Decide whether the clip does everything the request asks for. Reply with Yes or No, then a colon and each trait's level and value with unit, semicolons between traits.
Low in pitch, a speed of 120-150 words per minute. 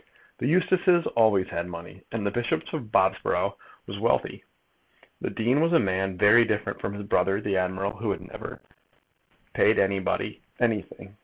No: low, 100 Hz; average, 160 wpm